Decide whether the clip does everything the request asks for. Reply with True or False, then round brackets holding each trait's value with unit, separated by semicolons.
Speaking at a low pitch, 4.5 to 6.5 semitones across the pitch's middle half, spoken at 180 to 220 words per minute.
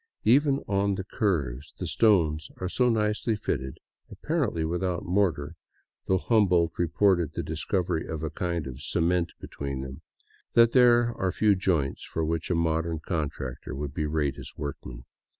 False (85 Hz; 4.9 semitones; 160 wpm)